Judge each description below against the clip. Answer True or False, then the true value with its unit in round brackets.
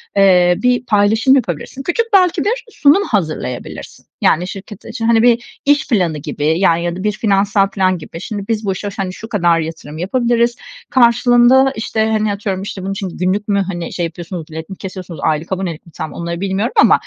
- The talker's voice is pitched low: False (200 Hz)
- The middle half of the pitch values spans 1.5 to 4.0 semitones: False (5.1 semitones)